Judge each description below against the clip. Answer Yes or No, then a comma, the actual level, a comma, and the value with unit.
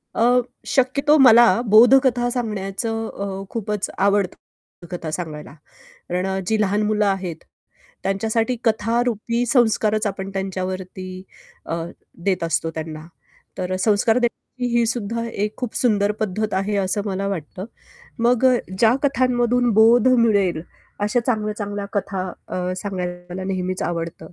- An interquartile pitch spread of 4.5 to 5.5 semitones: No, average, 3.8 semitones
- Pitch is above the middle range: Yes, high, 210 Hz